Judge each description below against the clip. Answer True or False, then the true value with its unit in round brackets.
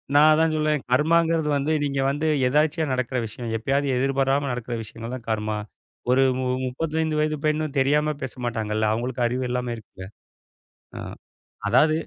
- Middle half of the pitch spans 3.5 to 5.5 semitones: True (3.9 semitones)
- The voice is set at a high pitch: False (135 Hz)